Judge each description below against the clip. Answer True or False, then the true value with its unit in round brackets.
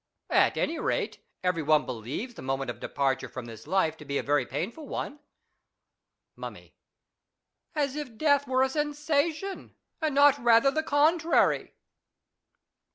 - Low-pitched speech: False (260 Hz)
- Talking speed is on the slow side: False (145 wpm)